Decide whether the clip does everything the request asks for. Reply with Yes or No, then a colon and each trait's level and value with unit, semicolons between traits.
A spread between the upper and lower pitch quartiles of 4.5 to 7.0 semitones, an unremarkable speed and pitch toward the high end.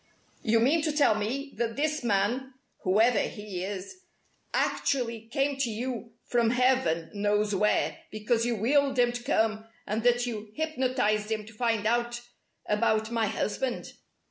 No: average, 3.2 semitones; average, 150 wpm; high, 230 Hz